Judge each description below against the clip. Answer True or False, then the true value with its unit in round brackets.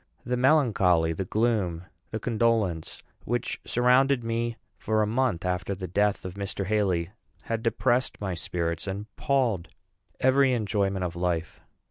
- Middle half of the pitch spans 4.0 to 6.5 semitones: True (4.8 semitones)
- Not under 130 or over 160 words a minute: True (140 wpm)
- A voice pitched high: False (105 Hz)